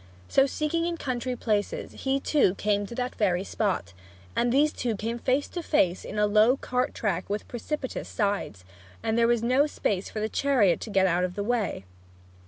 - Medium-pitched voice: No, high, 230 Hz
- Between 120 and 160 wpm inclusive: No, average, 195 wpm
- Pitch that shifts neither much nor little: Yes, average, 4.4 semitones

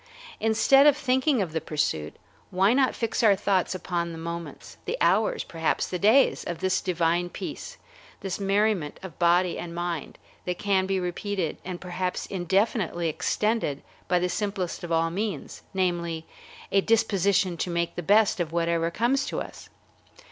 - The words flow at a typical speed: Yes, average, 160 wpm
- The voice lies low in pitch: No, medium, 185 Hz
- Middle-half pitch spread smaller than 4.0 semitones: Yes, average, 3.3 semitones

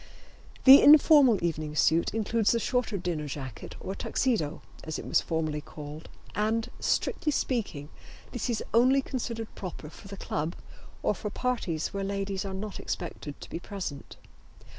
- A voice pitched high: Yes, high, 195 Hz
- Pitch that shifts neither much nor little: No, wide, 6.6 semitones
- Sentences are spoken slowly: No, average, 155 wpm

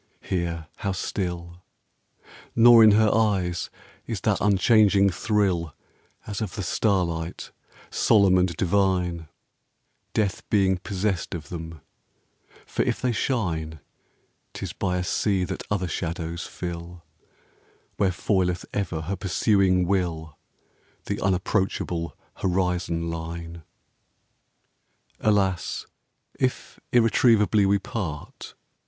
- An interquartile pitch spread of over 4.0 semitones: No, average, 3.0 semitones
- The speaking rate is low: Yes, slow, 110 wpm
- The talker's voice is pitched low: Yes, very low, 95 Hz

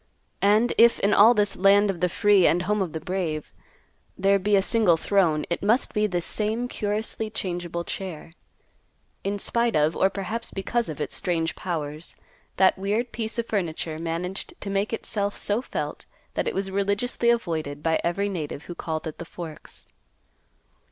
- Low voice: No, high, 195 Hz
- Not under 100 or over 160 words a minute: No, average, 175 wpm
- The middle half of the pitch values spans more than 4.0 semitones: No, average, 3.7 semitones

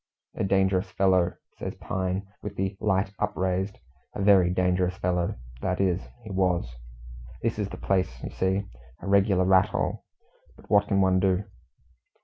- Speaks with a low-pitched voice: Yes, very low, 95 Hz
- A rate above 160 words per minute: No, average, 155 wpm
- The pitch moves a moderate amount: No, narrow, 1.1 semitones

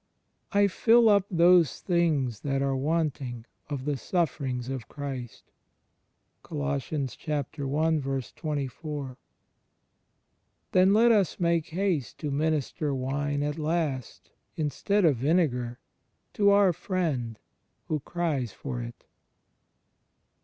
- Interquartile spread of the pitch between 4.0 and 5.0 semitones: Yes, average, 4.4 semitones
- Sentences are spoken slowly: Yes, slow, 105 wpm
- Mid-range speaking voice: Yes, medium, 150 Hz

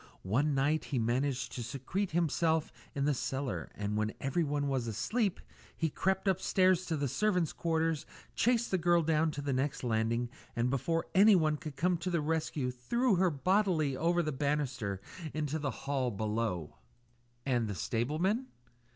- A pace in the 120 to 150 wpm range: No, average, 160 wpm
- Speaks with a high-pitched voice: No, medium, 150 Hz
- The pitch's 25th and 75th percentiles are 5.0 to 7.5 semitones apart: Yes, average, 5.3 semitones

